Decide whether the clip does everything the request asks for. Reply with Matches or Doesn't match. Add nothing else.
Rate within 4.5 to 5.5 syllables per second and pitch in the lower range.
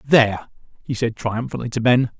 Matches